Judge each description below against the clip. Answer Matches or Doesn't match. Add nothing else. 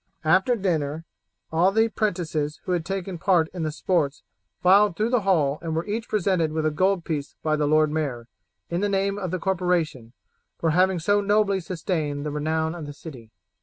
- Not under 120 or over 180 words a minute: Doesn't match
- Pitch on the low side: Doesn't match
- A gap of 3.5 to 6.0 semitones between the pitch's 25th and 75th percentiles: Matches